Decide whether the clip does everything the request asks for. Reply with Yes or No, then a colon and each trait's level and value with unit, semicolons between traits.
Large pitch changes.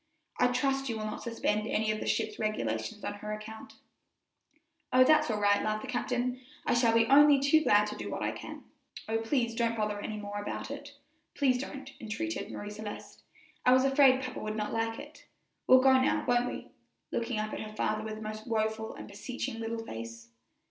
No: average, 3.2 semitones